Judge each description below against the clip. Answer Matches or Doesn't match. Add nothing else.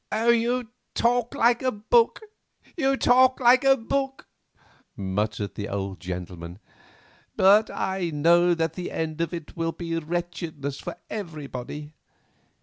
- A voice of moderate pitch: Matches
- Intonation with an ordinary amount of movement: Doesn't match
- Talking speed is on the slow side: Matches